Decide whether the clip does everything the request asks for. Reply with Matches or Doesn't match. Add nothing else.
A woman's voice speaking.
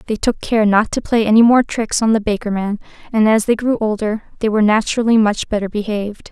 Matches